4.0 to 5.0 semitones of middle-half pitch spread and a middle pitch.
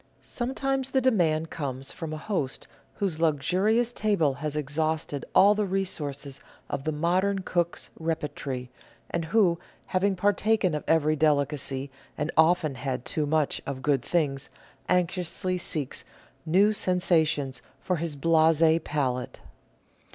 Yes: average, 4.3 semitones; medium, 160 Hz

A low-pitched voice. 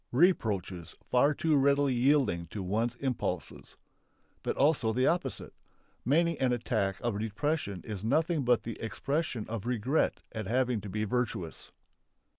Yes: low, 120 Hz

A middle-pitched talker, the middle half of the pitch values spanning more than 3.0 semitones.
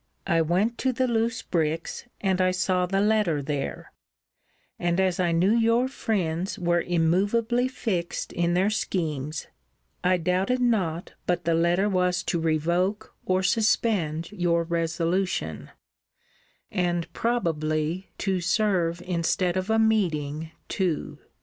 Yes: medium, 180 Hz; average, 3.7 semitones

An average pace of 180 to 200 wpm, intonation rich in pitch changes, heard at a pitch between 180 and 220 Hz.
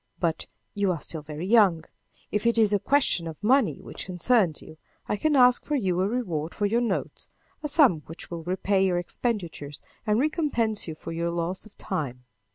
Yes: average, 195 wpm; wide, 5.8 semitones; high, 190 Hz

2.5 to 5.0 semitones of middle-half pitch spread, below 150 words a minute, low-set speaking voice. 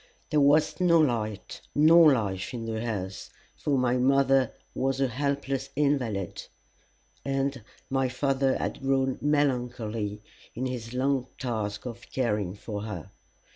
Yes: average, 3.8 semitones; slow, 135 wpm; low, 130 Hz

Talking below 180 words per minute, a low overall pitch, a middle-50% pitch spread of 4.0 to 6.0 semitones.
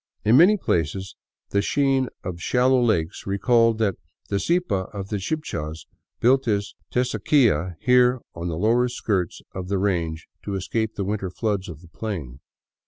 Yes: average, 160 wpm; low, 100 Hz; average, 5.1 semitones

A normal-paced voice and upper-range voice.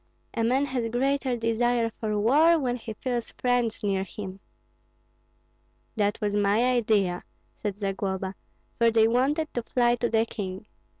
Yes: average, 145 wpm; high, 230 Hz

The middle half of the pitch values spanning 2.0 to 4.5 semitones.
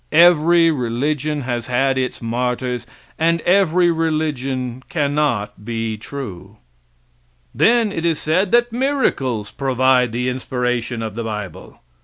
No: wide, 5.4 semitones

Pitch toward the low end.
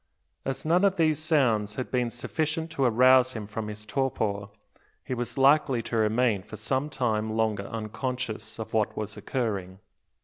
Yes: low, 120 Hz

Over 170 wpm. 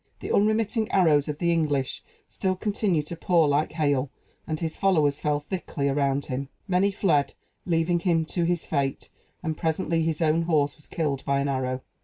Yes: average, 180 wpm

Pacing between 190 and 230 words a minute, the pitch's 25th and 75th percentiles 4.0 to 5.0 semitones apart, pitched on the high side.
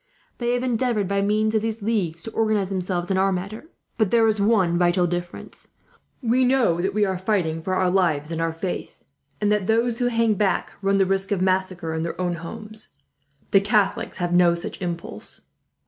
No: average, 200 wpm; average, 3.6 semitones; high, 195 Hz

